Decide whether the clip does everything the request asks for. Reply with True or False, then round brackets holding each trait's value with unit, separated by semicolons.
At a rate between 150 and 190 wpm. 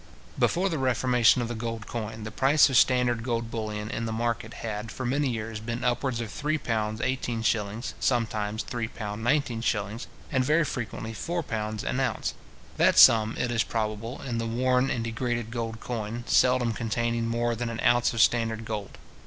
True (170 wpm)